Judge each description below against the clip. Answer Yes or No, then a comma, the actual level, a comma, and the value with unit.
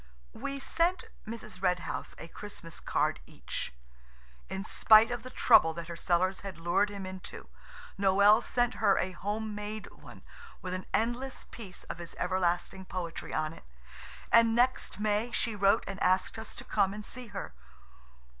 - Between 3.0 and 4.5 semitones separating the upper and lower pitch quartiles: Yes, average, 3.5 semitones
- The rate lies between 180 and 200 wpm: No, average, 165 wpm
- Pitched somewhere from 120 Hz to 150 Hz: No, high, 200 Hz